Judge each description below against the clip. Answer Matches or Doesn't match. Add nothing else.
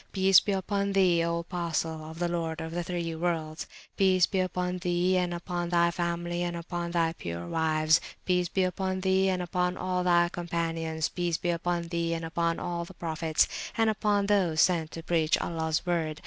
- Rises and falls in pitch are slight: Matches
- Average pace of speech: Matches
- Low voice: Doesn't match